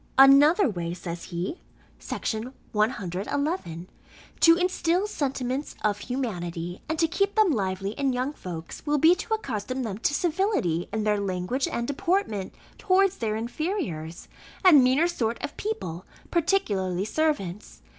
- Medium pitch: No, very high, 250 Hz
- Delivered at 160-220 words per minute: No, slow, 135 wpm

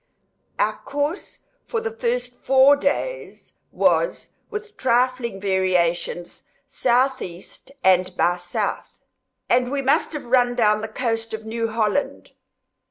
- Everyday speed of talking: No, slow, 120 wpm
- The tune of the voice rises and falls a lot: Yes, wide, 5.8 semitones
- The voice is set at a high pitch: Yes, high, 240 Hz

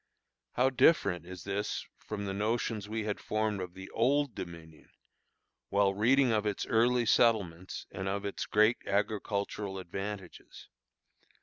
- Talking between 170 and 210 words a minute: No, slow, 135 wpm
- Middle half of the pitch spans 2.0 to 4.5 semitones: Yes, narrow, 2.6 semitones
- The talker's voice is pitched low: Yes, low, 105 Hz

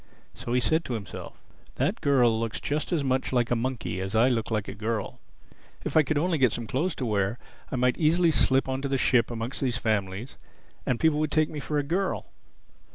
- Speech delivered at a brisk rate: Yes, fast, 220 wpm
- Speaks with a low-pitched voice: Yes, low, 130 Hz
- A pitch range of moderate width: Yes, average, 4.6 semitones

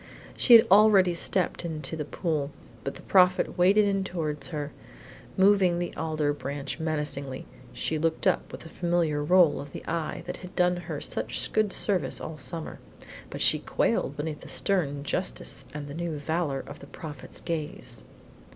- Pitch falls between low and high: Yes, medium, 160 Hz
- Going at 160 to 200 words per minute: Yes, average, 170 wpm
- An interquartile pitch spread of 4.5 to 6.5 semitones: No, average, 3.5 semitones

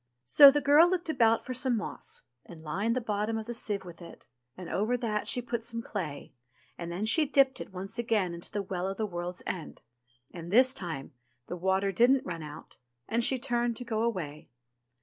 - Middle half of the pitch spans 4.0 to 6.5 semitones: Yes, average, 5.2 semitones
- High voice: Yes, high, 215 Hz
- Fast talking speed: Yes, fast, 210 wpm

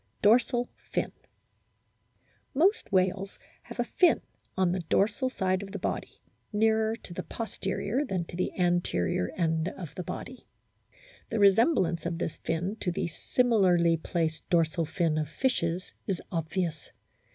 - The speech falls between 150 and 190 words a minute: No, average, 140 wpm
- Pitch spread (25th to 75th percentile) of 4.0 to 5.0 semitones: Yes, average, 4.5 semitones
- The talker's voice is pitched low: No, medium, 185 Hz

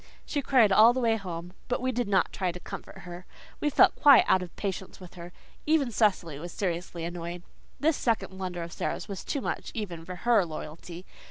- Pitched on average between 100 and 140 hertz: No, medium, 185 Hz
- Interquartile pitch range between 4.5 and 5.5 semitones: Yes, average, 5.1 semitones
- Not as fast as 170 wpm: No, fast, 205 wpm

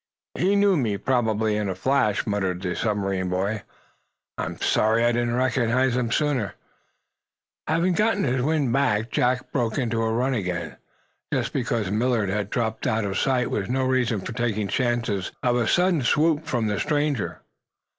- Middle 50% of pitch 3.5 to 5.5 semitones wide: Yes, average, 3.9 semitones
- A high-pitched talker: No, low, 120 Hz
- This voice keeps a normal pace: Yes, average, 165 wpm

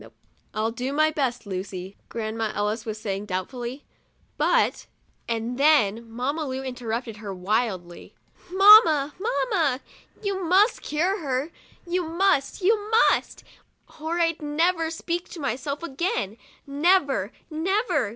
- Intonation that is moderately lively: No, wide, 7.2 semitones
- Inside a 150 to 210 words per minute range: No, average, 140 wpm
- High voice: Yes, very high, 275 Hz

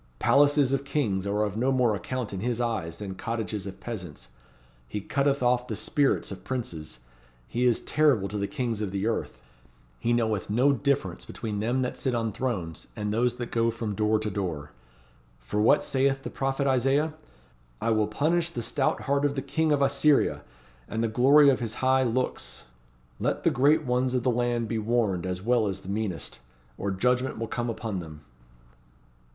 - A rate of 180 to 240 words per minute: Yes, average, 190 wpm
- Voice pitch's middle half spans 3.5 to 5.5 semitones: Yes, average, 4.1 semitones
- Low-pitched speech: Yes, low, 120 Hz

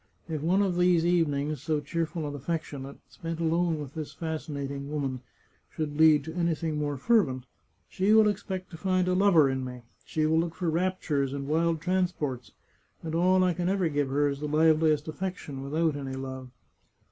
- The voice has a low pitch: No, medium, 160 Hz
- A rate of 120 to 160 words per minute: No, average, 185 wpm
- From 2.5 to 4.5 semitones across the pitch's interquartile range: Yes, average, 3.4 semitones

